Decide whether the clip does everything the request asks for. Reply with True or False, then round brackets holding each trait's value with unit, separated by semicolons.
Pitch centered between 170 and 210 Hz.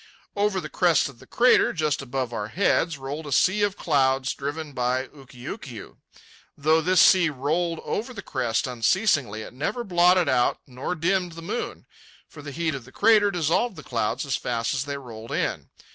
False (145 Hz)